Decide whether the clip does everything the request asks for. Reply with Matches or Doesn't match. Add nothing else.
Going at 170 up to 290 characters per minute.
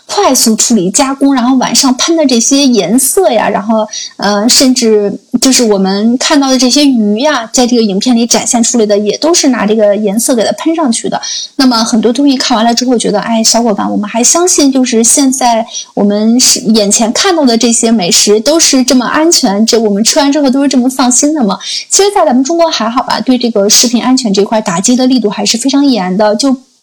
Doesn't match